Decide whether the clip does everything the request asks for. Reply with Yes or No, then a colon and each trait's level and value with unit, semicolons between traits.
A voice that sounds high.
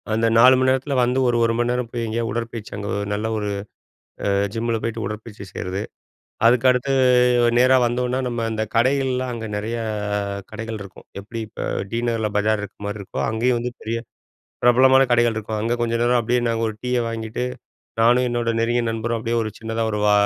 No: low, 115 Hz